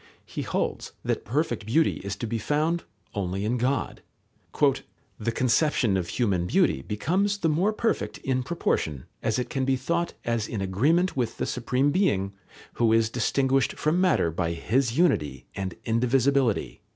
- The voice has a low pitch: Yes, low, 125 Hz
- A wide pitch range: Yes, wide, 6.5 semitones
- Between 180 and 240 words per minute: No, average, 160 wpm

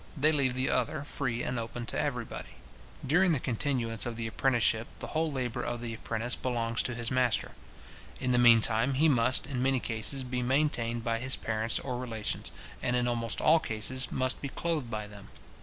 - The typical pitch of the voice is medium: No, low, 125 Hz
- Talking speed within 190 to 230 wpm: Yes, average, 195 wpm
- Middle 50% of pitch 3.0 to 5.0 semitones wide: No, narrow, 2.4 semitones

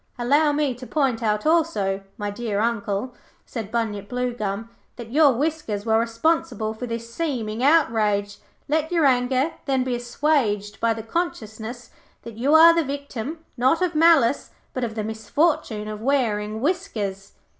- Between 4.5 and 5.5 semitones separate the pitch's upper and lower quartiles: Yes, average, 5.1 semitones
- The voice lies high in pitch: Yes, high, 240 Hz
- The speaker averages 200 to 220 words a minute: No, average, 155 wpm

